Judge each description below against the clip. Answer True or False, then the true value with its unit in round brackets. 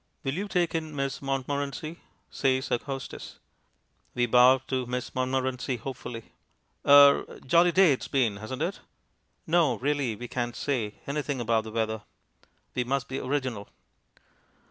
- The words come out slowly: False (145 wpm)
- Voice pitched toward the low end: True (130 Hz)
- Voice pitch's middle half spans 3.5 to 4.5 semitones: False (2.7 semitones)